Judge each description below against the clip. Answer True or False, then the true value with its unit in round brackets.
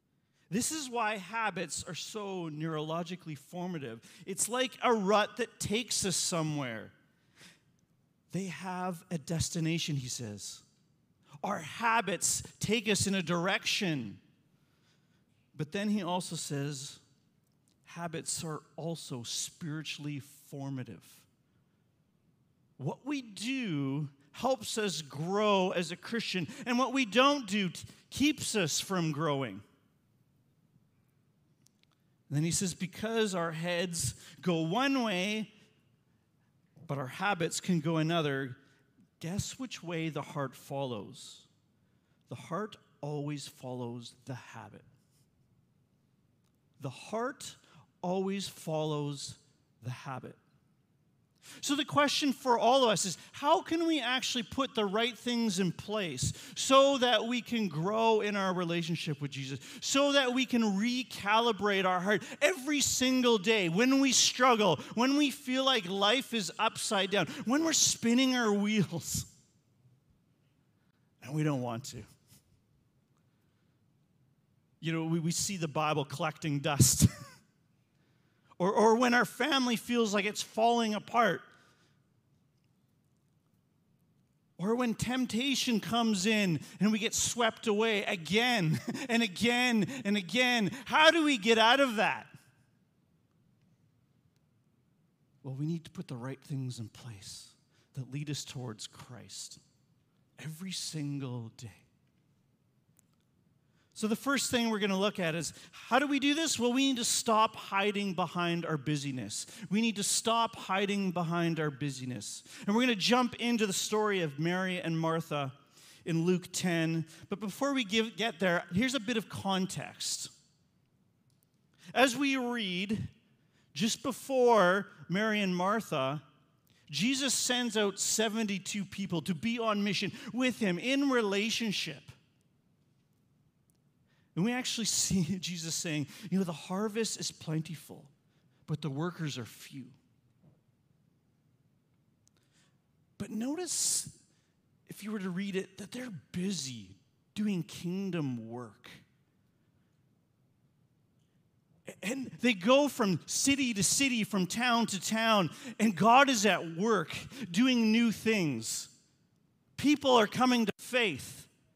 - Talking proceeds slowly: True (125 wpm)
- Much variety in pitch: True (7.2 semitones)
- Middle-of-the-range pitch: True (175 Hz)